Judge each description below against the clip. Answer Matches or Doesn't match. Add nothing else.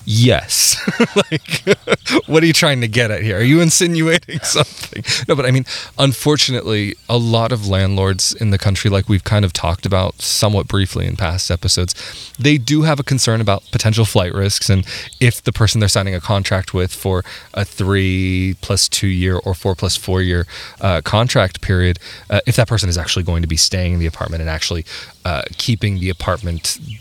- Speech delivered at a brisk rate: Doesn't match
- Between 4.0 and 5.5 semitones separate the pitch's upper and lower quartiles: Matches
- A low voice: Matches